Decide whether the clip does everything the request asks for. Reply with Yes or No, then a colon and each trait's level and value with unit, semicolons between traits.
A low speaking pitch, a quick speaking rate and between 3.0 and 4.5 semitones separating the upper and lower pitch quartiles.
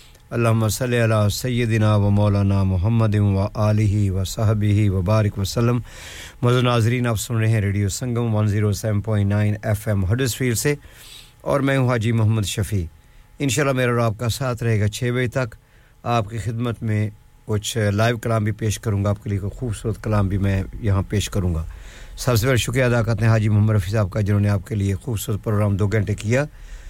No: low, 110 Hz; fast, 215 wpm; narrow, 2.6 semitones